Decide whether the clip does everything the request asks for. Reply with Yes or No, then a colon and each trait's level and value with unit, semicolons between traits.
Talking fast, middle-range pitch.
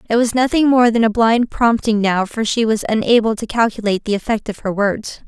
No: fast, 230 wpm; high, 220 Hz